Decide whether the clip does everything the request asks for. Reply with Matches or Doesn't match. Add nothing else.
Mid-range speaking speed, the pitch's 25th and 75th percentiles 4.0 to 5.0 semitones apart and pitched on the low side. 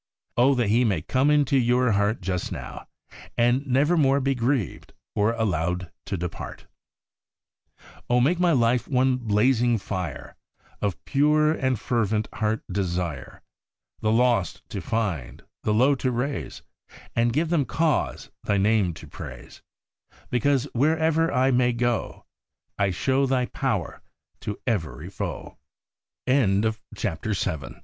Doesn't match